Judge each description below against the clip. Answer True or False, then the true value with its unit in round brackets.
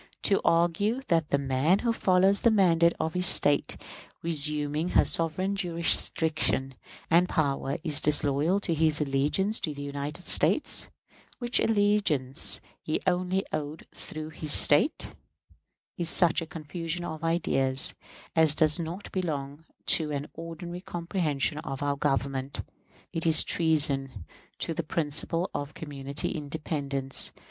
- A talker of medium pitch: True (160 Hz)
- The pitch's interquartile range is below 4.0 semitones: True (3.3 semitones)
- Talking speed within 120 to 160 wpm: True (135 wpm)